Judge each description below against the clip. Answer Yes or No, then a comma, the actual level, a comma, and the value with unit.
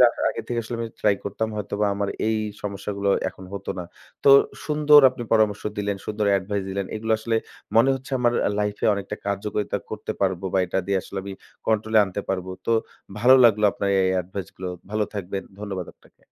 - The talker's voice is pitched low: Yes, low, 105 Hz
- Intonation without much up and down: Yes, narrow, 2.1 semitones